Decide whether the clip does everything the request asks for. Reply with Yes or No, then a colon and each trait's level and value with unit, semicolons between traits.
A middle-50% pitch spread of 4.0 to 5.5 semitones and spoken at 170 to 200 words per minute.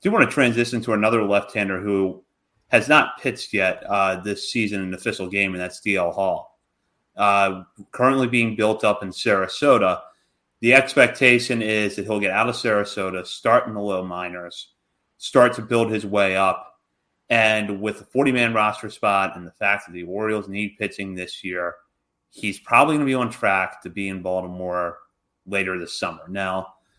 No: average, 2.7 semitones; average, 180 wpm